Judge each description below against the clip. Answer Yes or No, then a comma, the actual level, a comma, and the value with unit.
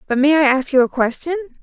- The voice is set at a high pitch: Yes, very high, 285 Hz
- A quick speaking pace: Yes, fast, 260 wpm